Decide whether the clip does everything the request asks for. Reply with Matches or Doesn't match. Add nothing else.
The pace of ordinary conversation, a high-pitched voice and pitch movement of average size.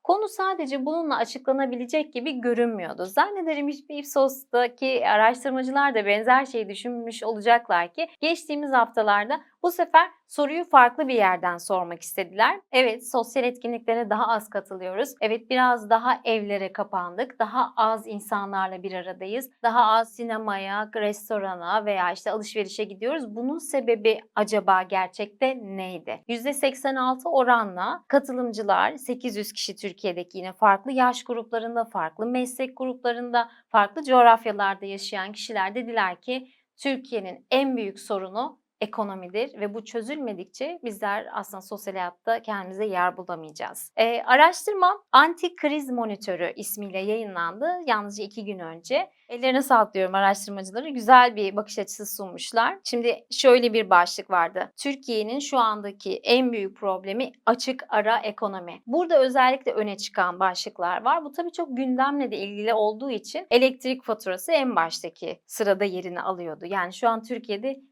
Matches